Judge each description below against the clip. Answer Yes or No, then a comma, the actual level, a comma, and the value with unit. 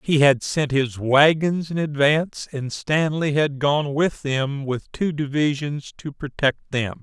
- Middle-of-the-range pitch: Yes, medium, 145 Hz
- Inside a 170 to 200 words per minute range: No, average, 160 wpm